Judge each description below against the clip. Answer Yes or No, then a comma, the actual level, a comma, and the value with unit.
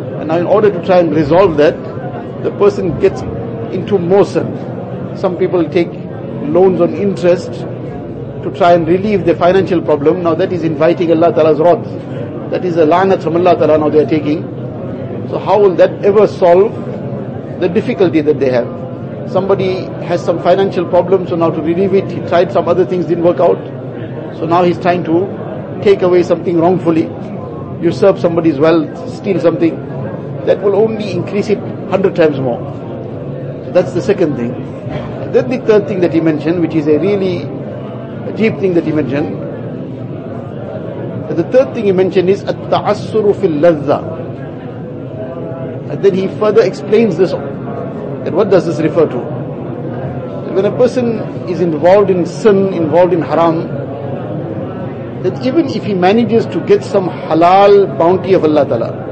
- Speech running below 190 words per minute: Yes, average, 165 wpm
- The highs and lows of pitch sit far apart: No, average, 3.6 semitones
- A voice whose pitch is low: No, medium, 170 Hz